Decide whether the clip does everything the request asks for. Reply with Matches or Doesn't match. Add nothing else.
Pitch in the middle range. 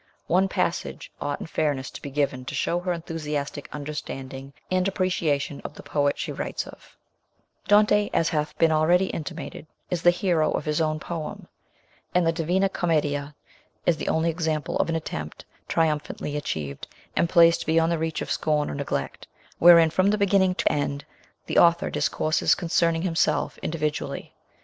Matches